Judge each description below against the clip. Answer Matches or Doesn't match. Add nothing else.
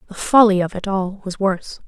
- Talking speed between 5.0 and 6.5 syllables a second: Matches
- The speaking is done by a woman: Matches